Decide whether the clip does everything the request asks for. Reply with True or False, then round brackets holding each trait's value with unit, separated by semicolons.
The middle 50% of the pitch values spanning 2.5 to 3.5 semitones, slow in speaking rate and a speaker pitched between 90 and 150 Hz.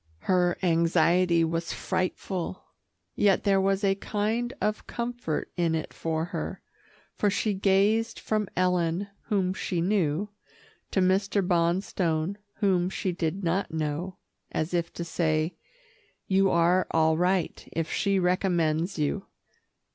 False (2.8 semitones; 130 wpm; 180 Hz)